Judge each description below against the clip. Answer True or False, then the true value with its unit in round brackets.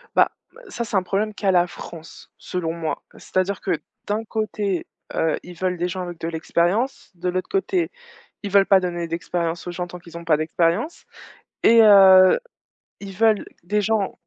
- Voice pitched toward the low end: False (185 Hz)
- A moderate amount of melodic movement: True (3.3 semitones)